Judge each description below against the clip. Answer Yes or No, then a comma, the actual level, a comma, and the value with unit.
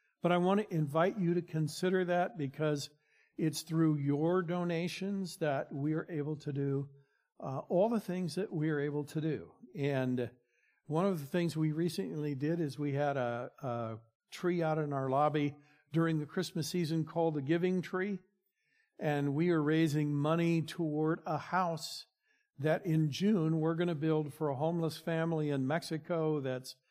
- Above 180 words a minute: No, average, 175 wpm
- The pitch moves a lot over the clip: No, average, 3.1 semitones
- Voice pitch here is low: No, medium, 160 Hz